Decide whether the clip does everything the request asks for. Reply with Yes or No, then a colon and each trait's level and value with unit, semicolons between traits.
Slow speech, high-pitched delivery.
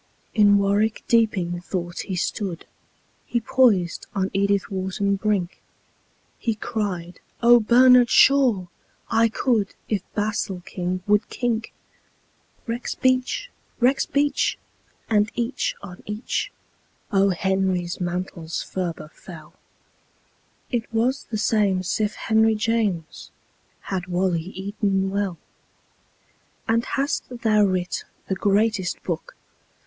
Yes: slow, 95 wpm; high, 205 Hz